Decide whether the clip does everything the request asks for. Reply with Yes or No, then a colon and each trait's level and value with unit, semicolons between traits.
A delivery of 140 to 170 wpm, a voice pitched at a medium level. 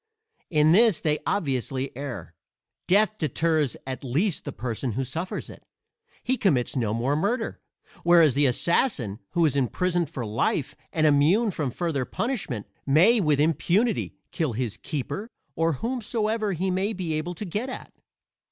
Yes: average, 150 wpm; medium, 160 Hz